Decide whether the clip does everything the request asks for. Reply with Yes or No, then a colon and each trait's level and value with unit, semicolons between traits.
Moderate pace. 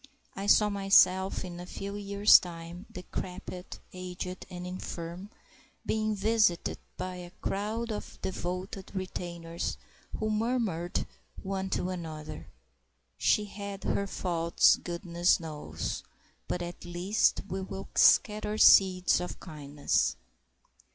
No: slow, 115 wpm